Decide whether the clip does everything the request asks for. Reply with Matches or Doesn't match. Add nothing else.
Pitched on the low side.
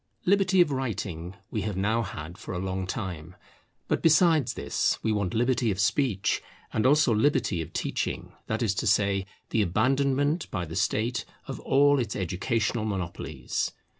Matches